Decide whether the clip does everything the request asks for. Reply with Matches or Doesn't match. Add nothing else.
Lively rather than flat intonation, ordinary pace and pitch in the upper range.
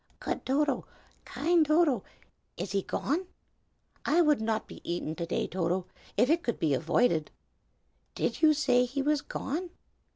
Matches